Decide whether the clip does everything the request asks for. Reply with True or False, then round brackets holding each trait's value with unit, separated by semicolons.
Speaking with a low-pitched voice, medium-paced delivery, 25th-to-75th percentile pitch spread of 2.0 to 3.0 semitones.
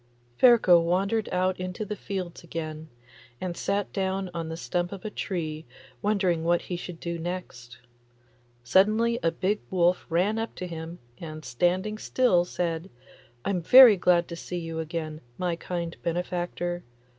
False (175 Hz; 155 wpm; 2.4 semitones)